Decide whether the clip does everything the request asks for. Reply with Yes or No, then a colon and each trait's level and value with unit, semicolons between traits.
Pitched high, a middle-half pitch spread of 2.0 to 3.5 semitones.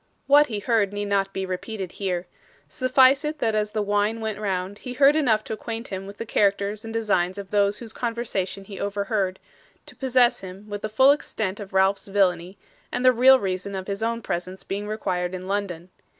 Yes: high, 205 Hz; average, 2.9 semitones